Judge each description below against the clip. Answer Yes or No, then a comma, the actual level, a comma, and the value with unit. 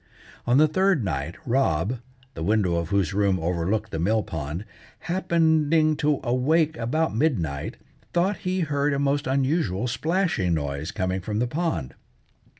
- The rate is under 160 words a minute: Yes, average, 150 wpm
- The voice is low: Yes, low, 120 Hz